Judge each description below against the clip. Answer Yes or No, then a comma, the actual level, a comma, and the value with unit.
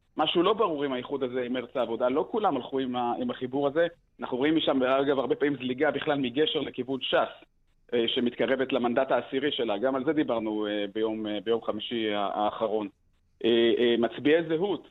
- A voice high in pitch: No, low, 130 Hz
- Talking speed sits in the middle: No, fast, 160 wpm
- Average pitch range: Yes, average, 3.6 semitones